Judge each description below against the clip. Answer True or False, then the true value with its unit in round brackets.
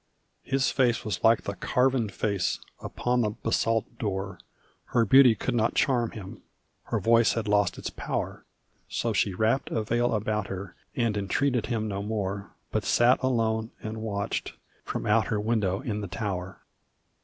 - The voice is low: True (110 Hz)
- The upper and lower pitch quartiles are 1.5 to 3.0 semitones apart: True (2.7 semitones)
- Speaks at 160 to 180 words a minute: True (165 wpm)